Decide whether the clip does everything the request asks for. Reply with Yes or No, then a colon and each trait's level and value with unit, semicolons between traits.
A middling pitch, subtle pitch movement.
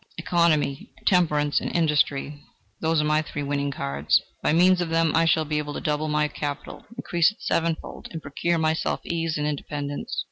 Yes: medium, 155 Hz; narrow, 2.1 semitones